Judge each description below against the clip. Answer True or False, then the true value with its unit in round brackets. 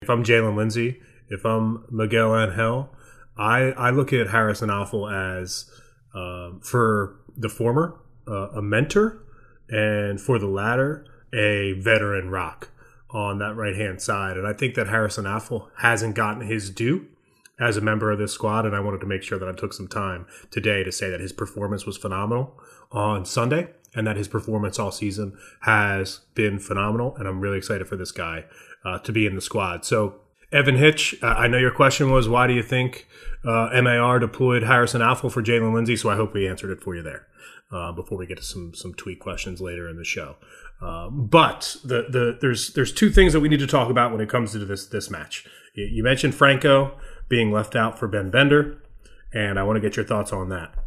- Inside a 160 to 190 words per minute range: False (205 wpm)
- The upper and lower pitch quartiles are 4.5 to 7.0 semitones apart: False (3.5 semitones)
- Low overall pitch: True (110 Hz)